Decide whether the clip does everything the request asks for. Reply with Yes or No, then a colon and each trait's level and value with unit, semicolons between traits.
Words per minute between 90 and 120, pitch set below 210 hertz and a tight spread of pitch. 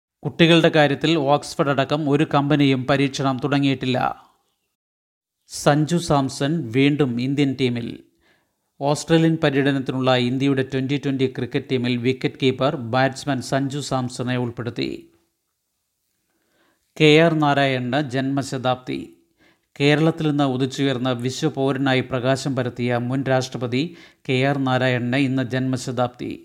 Yes: average, 100 wpm; low, 135 Hz; narrow, 2.1 semitones